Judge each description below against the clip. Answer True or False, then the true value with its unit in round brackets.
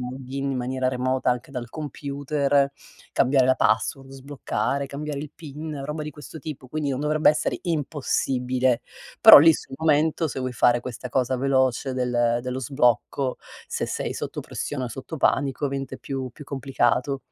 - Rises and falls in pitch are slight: True (2.3 semitones)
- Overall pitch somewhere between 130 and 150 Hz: True (135 Hz)